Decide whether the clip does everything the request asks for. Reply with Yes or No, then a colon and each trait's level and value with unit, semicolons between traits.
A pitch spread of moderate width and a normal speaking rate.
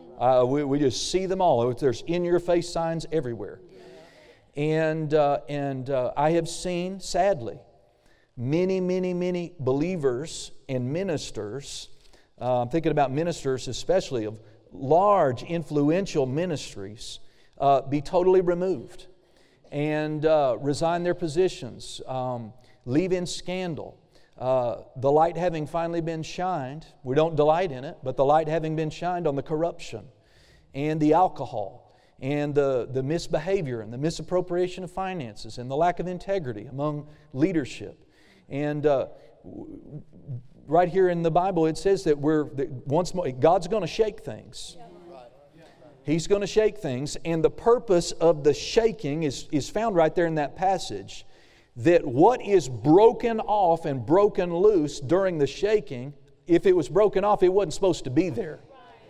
Yes: average, 4.6 semitones; average, 150 wpm